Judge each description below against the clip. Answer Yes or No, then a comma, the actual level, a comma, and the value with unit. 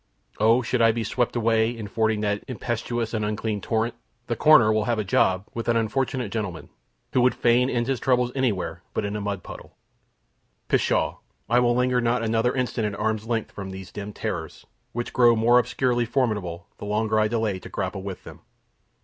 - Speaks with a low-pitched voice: Yes, low, 115 Hz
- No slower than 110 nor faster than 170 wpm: No, average, 195 wpm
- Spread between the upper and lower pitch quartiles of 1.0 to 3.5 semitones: Yes, narrow, 2.6 semitones